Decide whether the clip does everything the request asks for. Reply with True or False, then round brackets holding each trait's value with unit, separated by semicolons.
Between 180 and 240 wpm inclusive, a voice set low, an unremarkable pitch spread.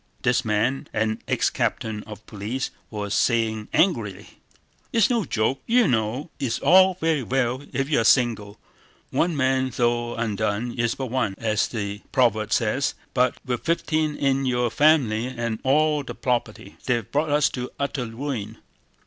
False (155 wpm; 125 Hz; 4.1 semitones)